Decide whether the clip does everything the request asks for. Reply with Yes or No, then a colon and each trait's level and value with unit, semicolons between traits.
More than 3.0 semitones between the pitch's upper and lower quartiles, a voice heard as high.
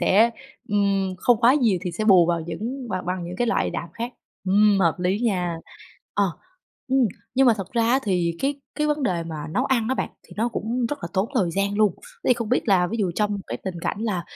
Yes: average, 4.6 semitones; high, 205 Hz